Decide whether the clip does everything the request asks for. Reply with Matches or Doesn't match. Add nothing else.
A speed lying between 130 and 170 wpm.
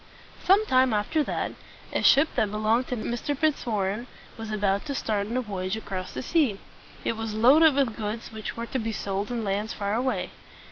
Doesn't match